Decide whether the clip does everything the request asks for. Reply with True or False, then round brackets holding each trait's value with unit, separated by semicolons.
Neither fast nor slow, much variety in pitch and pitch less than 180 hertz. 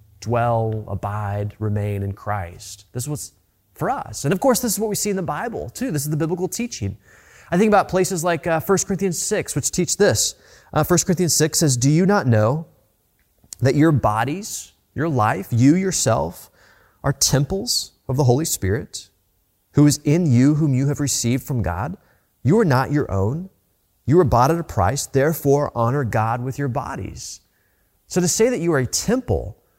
True (195 wpm; 8.1 semitones; 140 Hz)